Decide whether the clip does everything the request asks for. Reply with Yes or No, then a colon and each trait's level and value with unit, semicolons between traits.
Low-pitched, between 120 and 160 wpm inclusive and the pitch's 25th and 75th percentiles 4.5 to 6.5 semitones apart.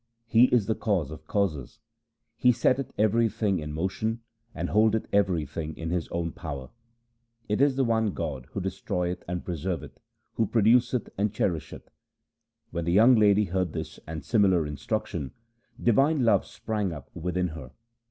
Yes: very low, 95 Hz; average, 155 wpm; average, 5.2 semitones